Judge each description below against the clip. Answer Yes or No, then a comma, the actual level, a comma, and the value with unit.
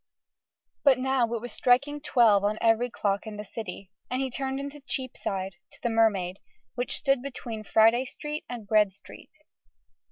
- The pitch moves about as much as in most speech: Yes, average, 3.9 semitones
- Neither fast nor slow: Yes, average, 165 wpm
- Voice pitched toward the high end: Yes, high, 235 Hz